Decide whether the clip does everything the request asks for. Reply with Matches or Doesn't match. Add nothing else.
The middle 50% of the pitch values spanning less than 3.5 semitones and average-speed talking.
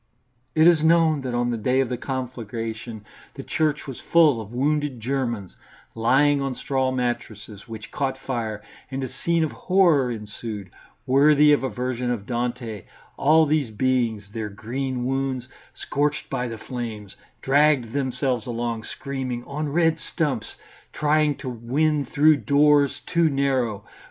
Doesn't match